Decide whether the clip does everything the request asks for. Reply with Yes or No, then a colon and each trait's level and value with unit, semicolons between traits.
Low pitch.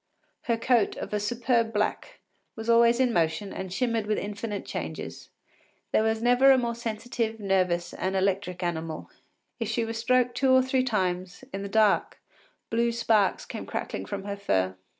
No: high, 220 Hz